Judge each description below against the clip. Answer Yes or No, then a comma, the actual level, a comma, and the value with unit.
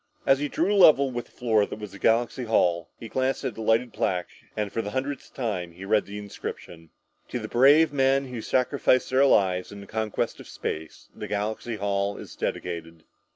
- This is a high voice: No, low, 110 Hz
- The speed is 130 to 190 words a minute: No, average, 200 wpm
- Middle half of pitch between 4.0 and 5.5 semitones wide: Yes, average, 4.7 semitones